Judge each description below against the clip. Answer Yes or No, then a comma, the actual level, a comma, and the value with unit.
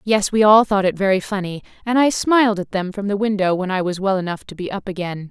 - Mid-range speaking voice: No, high, 200 Hz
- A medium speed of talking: No, fast, 270 wpm